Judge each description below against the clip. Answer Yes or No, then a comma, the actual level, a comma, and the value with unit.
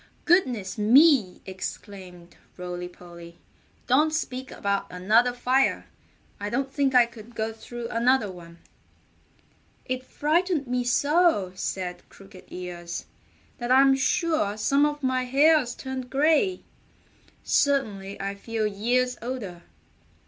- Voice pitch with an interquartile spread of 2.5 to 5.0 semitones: No, wide, 5.6 semitones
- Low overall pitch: No, high, 240 Hz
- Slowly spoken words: Yes, slow, 120 wpm